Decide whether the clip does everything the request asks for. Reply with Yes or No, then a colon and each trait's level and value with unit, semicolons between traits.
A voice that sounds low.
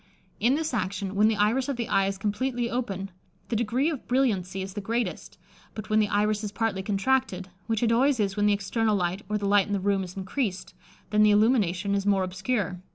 No: high, 210 Hz